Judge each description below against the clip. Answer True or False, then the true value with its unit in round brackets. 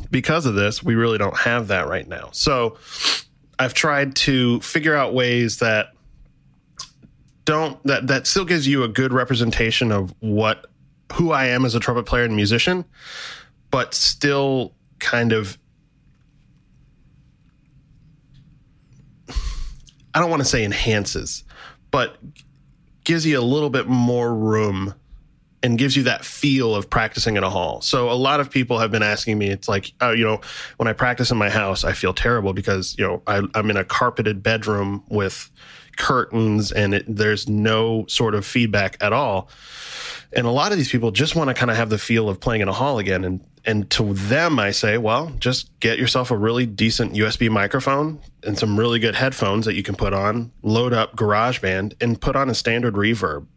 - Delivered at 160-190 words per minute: True (180 wpm)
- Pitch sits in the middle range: False (115 Hz)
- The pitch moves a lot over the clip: False (4.0 semitones)